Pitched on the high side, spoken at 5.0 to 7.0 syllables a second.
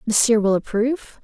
Yes: high, 225 Hz; 5.6 syllables/s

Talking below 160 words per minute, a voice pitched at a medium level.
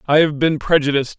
No: fast, 205 wpm; medium, 150 Hz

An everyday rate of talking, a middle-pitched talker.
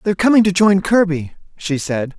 Yes: average, 195 wpm; medium, 180 Hz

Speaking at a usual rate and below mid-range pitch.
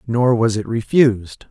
Yes: average, 160 wpm; low, 115 Hz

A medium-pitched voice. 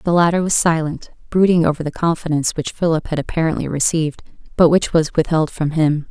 Yes: medium, 160 Hz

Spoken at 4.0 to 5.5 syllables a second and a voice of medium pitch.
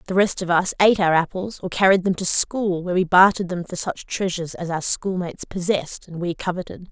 No: 6.0 syllables/s; medium, 180 Hz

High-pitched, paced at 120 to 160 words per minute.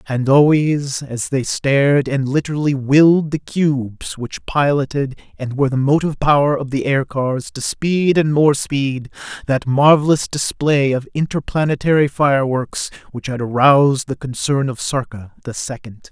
No: medium, 140 Hz; average, 150 wpm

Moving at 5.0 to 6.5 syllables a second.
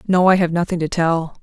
Yes: 5.6 syllables/s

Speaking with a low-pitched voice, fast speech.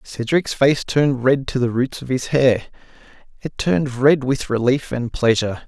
No: low, 130 Hz; average, 180 wpm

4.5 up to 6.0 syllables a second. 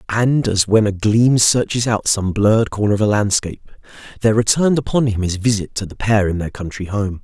Yes: 5.6 syllables/s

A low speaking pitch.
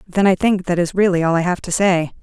No: medium, 180 Hz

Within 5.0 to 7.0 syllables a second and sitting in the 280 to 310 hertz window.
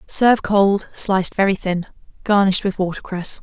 No: 5.1 syllables/s; high, 195 Hz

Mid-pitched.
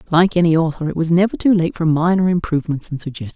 Yes: medium, 170 Hz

